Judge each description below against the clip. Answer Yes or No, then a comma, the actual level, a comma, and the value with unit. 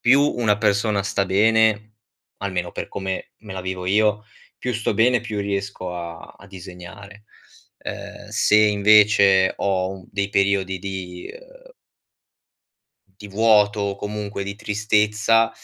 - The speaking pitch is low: Yes, low, 100 Hz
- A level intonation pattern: Yes, narrow, 2.0 semitones